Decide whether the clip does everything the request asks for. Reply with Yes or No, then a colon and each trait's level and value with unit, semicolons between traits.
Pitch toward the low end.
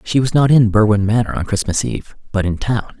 Yes: low, 110 Hz